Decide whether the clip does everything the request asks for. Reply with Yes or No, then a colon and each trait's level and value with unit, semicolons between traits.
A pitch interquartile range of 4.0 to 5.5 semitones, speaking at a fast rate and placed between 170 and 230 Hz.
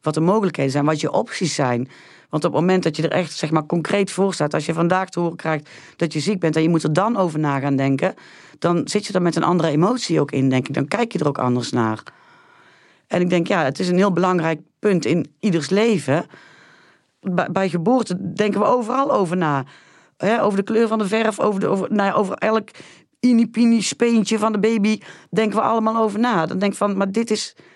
Yes: average, 5.1 semitones; fast, 240 wpm; medium, 185 Hz